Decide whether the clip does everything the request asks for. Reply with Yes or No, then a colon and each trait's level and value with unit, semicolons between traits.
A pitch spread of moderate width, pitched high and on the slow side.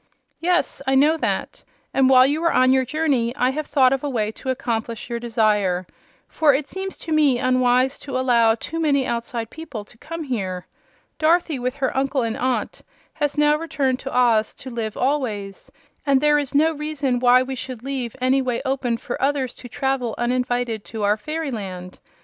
No: average, 3.4 semitones; very high, 255 Hz; average, 190 wpm